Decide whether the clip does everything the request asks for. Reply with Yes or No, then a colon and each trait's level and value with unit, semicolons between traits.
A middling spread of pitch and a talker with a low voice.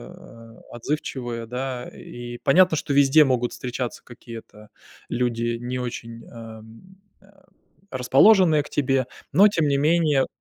Yes: average, 3.7 semitones; low, 125 Hz